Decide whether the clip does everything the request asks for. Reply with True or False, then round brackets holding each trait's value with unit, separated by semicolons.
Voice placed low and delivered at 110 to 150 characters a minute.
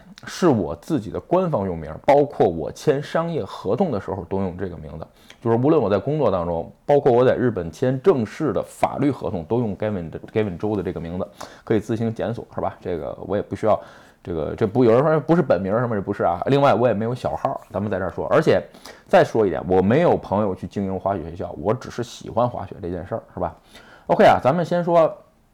False (110 Hz; 360 characters per minute)